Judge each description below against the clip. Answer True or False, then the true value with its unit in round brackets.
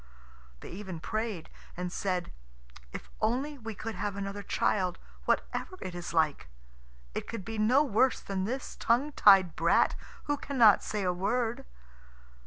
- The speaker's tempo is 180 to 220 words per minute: False (150 wpm)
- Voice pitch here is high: True (210 Hz)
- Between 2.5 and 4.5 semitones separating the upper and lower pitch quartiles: True (4.1 semitones)